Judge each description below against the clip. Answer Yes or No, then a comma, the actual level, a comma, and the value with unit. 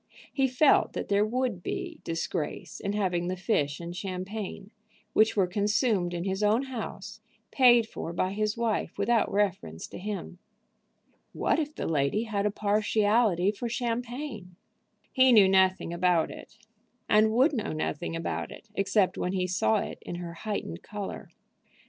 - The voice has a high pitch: Yes, high, 205 Hz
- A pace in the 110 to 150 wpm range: No, average, 160 wpm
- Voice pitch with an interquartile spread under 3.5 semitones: No, average, 4.0 semitones